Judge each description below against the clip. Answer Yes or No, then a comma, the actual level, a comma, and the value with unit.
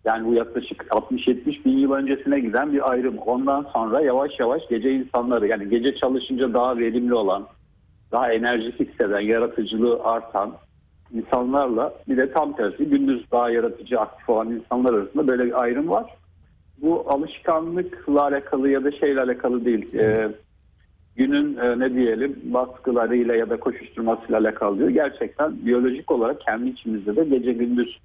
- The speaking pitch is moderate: No, low, 125 Hz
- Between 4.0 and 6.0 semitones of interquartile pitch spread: No, average, 3.4 semitones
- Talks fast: Yes, fast, 150 wpm